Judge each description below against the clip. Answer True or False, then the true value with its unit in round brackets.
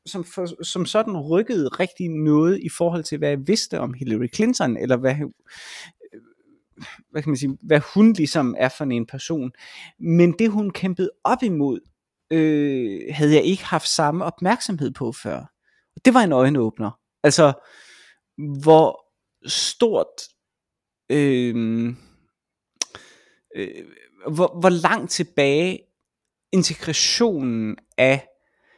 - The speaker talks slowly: True (120 wpm)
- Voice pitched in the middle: True (160 Hz)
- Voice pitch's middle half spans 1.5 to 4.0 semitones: False (5.1 semitones)